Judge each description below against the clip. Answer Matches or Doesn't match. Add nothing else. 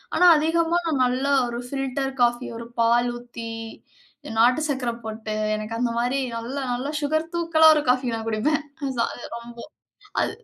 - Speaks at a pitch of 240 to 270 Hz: Matches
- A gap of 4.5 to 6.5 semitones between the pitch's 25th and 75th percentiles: Doesn't match